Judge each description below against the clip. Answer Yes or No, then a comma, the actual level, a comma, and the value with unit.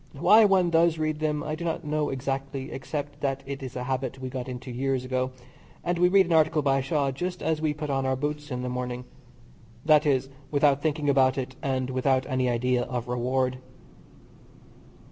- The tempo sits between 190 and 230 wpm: Yes, average, 200 wpm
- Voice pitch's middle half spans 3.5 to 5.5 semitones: No, average, 2.9 semitones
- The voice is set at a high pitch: No, low, 135 Hz